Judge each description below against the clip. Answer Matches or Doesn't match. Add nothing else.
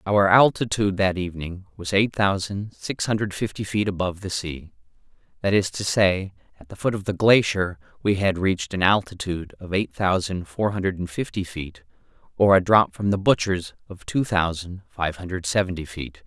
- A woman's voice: Doesn't match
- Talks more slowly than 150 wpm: Doesn't match